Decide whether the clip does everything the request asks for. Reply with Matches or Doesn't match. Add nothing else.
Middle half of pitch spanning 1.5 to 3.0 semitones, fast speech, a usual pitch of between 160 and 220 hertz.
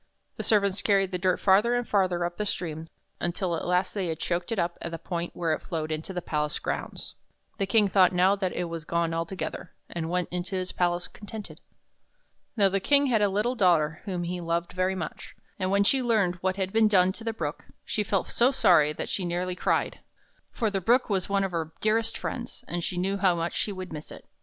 Matches